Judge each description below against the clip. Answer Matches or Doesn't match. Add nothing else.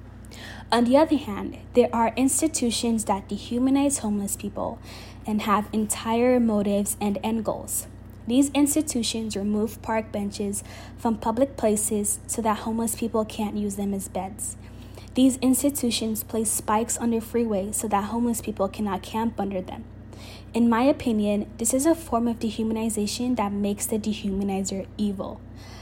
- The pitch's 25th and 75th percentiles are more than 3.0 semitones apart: Doesn't match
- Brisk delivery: Doesn't match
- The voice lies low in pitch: Doesn't match